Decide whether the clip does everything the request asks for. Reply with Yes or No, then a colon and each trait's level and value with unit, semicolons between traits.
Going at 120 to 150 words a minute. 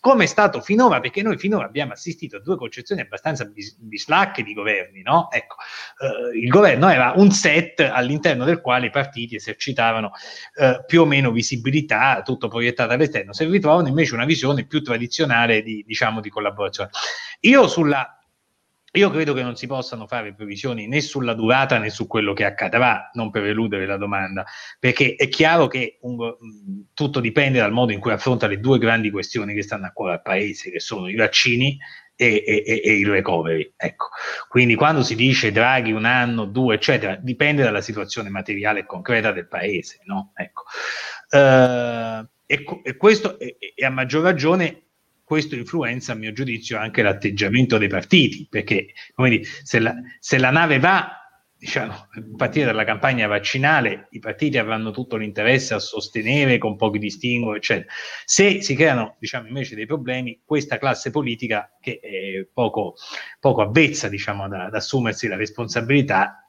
No: fast, 170 wpm